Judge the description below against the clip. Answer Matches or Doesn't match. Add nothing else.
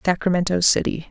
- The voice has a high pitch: Doesn't match